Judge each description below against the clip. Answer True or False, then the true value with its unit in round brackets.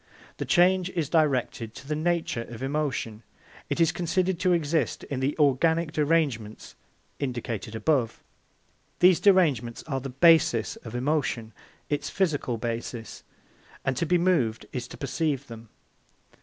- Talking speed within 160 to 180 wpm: False (140 wpm)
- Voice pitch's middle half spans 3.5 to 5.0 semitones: False (5.6 semitones)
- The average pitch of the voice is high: False (145 Hz)